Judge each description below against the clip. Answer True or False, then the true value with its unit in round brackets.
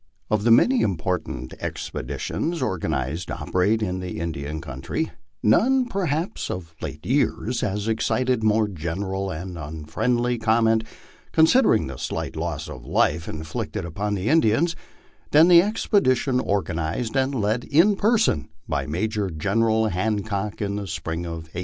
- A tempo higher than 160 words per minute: False (140 wpm)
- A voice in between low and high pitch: False (105 Hz)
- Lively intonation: True (6.8 semitones)